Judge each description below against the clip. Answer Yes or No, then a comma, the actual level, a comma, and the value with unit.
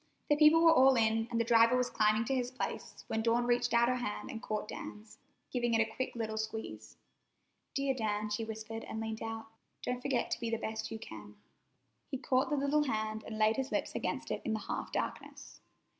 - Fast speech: Yes, fast, 220 wpm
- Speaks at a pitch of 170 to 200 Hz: No, high, 230 Hz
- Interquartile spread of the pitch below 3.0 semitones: Yes, narrow, 2.4 semitones